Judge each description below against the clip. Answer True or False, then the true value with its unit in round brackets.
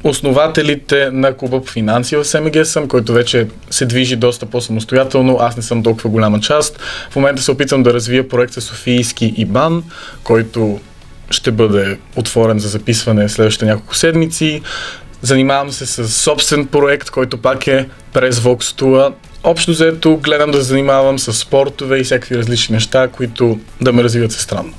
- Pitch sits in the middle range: False (130 Hz)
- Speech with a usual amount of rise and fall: True (3.4 semitones)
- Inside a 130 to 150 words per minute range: False (165 wpm)